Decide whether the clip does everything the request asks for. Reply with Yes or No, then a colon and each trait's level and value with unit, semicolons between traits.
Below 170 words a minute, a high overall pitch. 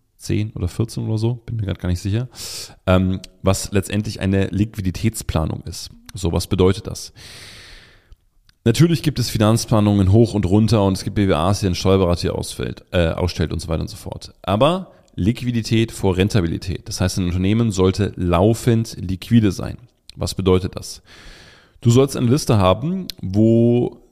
No: average, 160 wpm; low, 105 Hz